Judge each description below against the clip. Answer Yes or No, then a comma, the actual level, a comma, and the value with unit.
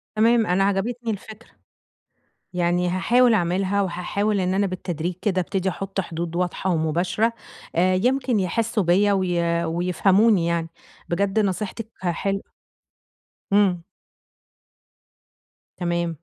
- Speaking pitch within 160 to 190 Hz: Yes, medium, 185 Hz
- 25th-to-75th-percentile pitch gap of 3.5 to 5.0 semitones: No, average, 2.9 semitones